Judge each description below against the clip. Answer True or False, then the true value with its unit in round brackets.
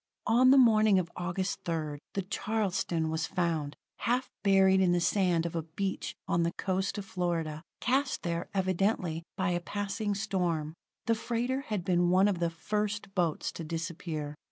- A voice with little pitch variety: False (3.4 semitones)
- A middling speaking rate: True (170 wpm)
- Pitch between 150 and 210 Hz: True (185 Hz)